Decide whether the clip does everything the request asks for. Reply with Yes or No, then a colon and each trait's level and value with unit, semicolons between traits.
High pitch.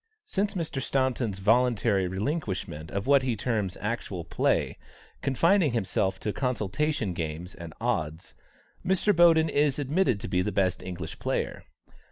No: low, 115 Hz